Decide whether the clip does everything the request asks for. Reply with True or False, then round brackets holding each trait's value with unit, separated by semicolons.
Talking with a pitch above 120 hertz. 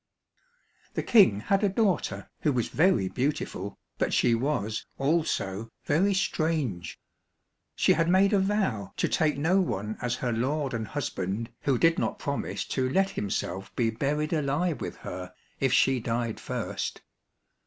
True (135 Hz)